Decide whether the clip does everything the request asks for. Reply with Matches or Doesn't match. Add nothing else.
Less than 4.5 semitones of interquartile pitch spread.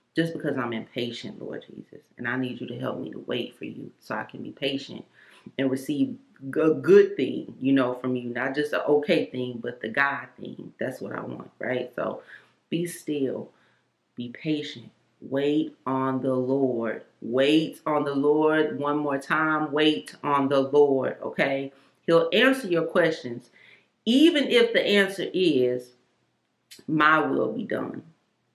Matches